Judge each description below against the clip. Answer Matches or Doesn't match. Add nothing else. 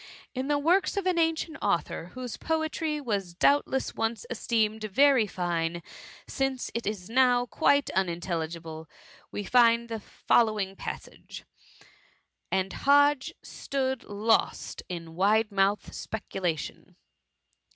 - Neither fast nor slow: Doesn't match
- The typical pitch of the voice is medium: Doesn't match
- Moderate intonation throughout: Doesn't match